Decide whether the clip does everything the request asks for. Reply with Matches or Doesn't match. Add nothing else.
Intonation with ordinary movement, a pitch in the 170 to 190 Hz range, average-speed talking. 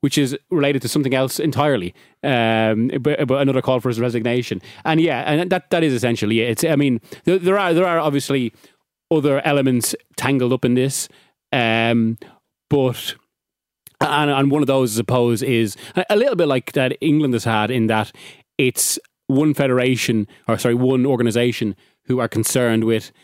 Doesn't match